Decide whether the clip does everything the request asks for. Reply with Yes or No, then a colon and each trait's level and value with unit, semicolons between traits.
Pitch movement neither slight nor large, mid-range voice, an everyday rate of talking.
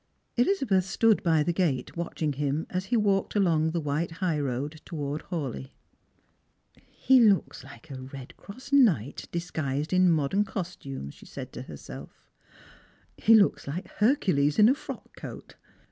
No: wide, 5.7 semitones; medium, 165 Hz; average, 160 wpm